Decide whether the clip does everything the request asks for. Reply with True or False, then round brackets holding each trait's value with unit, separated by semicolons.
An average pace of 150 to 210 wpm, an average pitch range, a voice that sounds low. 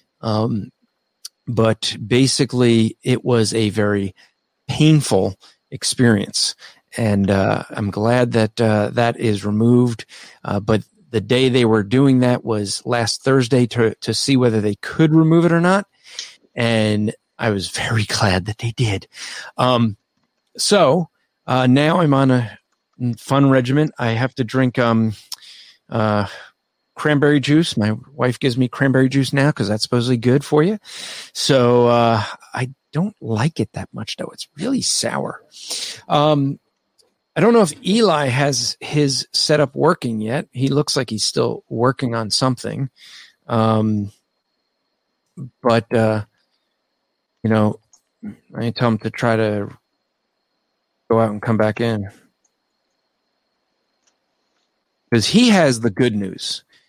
False (140 wpm; 3.6 semitones; 120 Hz)